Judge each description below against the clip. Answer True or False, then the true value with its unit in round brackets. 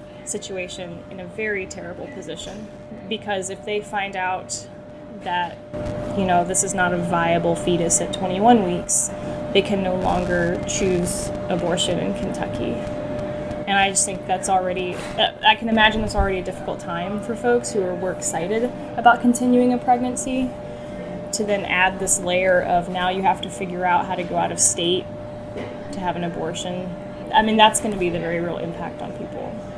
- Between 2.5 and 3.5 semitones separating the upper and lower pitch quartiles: True (2.9 semitones)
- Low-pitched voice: False (195 Hz)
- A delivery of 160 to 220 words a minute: True (180 wpm)